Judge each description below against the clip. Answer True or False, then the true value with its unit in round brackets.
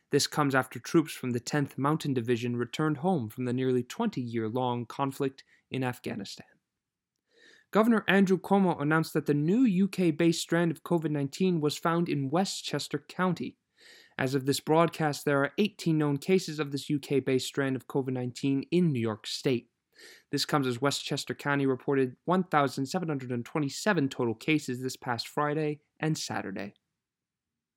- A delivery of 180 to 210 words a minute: False (160 wpm)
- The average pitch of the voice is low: False (145 Hz)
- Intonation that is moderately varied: True (4.3 semitones)